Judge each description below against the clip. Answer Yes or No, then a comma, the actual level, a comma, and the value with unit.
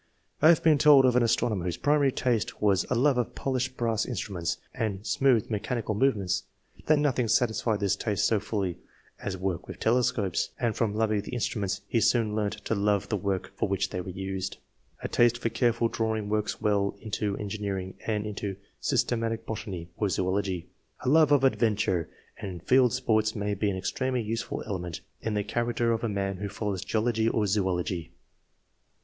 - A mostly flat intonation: No, average, 3.2 semitones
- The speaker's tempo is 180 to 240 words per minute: Yes, average, 185 wpm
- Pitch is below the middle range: Yes, low, 105 Hz